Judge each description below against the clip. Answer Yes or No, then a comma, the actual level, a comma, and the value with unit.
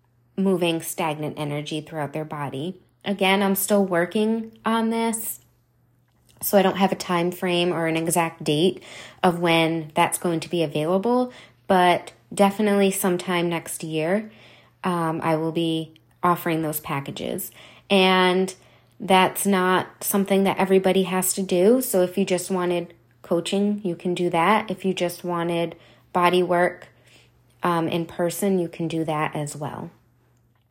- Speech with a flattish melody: No, average, 3.0 semitones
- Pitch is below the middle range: No, medium, 175 Hz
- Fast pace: No, average, 150 wpm